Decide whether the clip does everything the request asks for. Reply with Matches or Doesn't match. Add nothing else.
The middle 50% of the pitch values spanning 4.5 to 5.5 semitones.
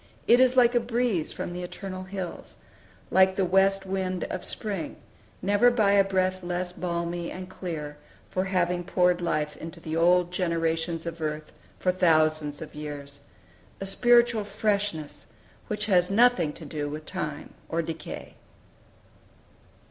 Doesn't match